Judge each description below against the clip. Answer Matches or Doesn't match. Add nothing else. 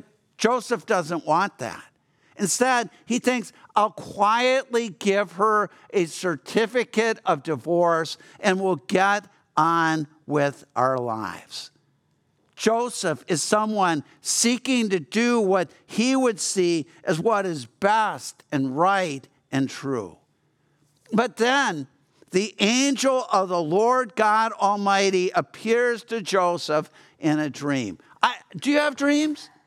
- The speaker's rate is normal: Doesn't match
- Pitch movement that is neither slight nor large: Doesn't match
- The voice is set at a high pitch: Matches